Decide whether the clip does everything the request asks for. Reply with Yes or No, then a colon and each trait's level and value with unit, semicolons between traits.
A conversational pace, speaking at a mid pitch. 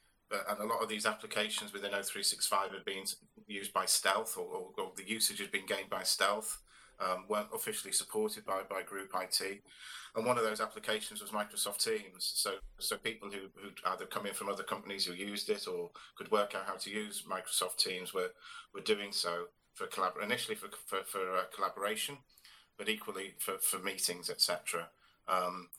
No: average, 190 wpm; low, 115 Hz